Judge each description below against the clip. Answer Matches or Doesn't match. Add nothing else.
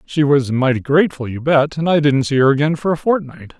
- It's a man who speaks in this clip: Matches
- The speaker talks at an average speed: Doesn't match